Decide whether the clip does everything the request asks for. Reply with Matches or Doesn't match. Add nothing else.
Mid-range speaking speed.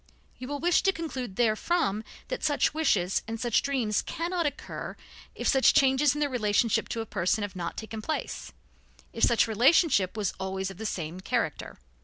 Matches